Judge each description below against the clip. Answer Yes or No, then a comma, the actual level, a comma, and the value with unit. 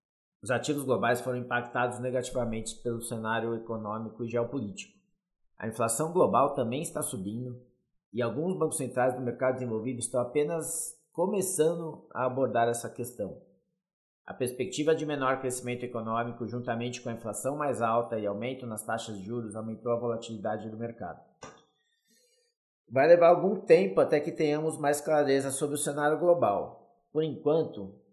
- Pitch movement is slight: No, average, 4.8 semitones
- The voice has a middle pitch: No, low, 125 Hz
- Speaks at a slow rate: No, average, 145 wpm